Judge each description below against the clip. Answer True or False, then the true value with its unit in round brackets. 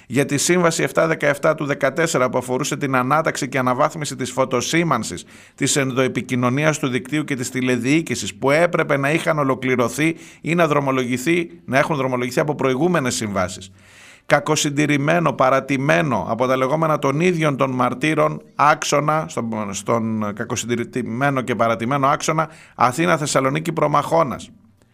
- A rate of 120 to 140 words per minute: True (125 wpm)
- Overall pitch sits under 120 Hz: False (140 Hz)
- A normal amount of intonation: True (3.5 semitones)